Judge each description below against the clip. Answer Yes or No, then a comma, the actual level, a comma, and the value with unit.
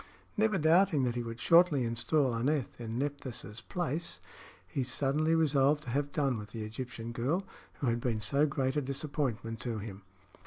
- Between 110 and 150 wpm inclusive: No, average, 170 wpm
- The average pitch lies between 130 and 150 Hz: Yes, low, 135 Hz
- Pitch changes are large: No, average, 4.4 semitones